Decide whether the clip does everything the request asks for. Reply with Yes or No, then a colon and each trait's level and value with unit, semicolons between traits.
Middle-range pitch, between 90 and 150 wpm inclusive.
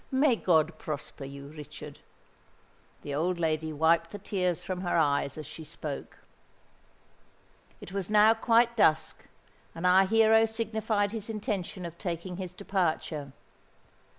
Yes: medium, 180 Hz; slow, 135 wpm